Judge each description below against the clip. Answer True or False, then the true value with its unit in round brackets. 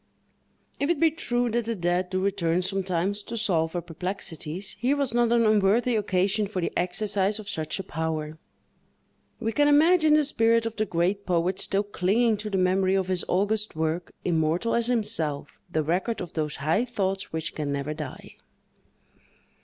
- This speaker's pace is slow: False (175 wpm)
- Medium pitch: False (195 Hz)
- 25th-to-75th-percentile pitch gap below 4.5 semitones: False (4.9 semitones)